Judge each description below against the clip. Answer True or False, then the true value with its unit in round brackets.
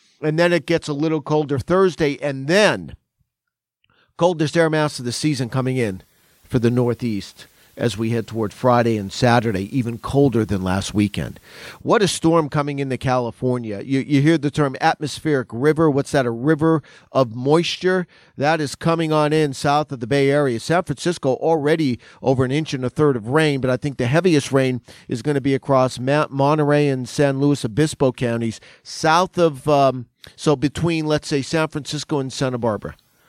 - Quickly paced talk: False (185 wpm)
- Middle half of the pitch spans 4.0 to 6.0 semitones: False (3.5 semitones)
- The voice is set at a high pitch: False (140 Hz)